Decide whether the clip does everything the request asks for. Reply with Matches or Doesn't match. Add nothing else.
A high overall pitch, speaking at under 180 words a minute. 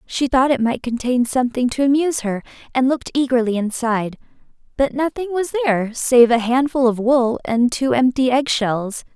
Matches